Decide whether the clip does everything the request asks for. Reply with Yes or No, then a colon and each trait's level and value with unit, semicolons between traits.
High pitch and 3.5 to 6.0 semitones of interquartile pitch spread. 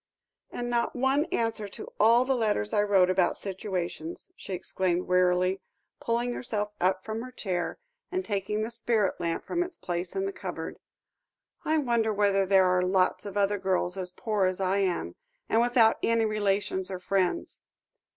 Yes: high, 200 Hz; average, 3.8 semitones